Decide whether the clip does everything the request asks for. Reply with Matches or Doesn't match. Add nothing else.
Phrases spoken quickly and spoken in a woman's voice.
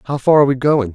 Doesn't match